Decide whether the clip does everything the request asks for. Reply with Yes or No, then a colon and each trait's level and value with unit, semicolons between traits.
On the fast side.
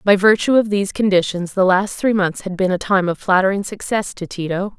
Yes: fast, 225 wpm